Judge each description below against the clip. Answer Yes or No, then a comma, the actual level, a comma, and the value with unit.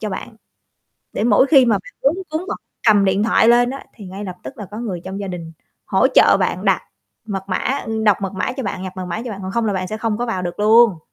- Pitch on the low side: No, high, 210 Hz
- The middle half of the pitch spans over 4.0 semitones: No, average, 3.7 semitones